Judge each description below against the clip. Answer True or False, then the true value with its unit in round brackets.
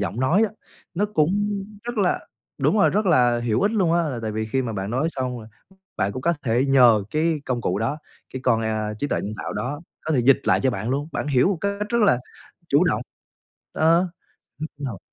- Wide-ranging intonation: True (6.6 semitones)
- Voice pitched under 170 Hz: True (135 Hz)